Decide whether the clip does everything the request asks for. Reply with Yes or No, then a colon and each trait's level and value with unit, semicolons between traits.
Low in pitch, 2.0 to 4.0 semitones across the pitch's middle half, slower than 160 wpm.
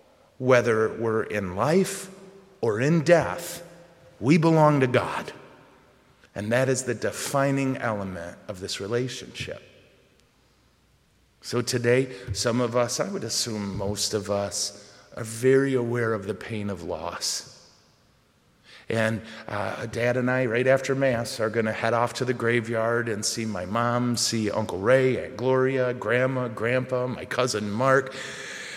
Yes: low, 120 Hz; average, 3.1 semitones; average, 145 wpm